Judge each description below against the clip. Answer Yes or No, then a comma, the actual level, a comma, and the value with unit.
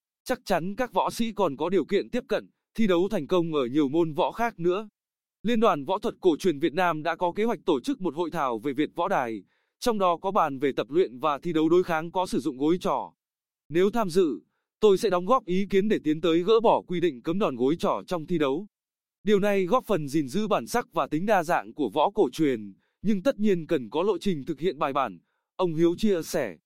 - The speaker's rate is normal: No, fast, 255 wpm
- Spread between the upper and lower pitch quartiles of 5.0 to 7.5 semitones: No, average, 4.4 semitones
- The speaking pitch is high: No, medium, 180 Hz